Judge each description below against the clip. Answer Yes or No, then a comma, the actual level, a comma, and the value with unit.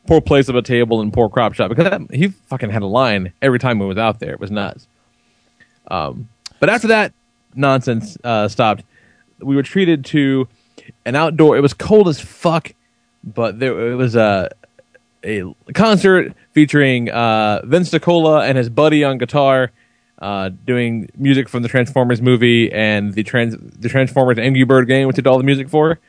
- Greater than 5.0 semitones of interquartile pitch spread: No, average, 3.7 semitones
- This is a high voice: No, low, 130 Hz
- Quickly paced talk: No, average, 185 wpm